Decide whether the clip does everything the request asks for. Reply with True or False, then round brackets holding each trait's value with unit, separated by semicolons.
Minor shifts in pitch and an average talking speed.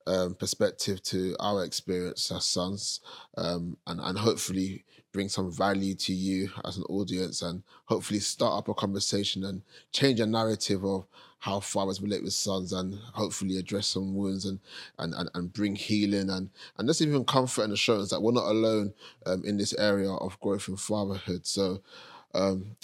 True (1.6 semitones; 175 wpm)